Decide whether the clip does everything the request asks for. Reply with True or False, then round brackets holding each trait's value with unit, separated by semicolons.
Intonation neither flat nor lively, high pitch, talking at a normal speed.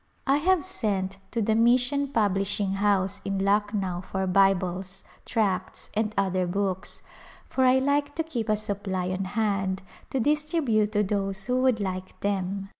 True (3.9 semitones; 205 Hz; 155 wpm)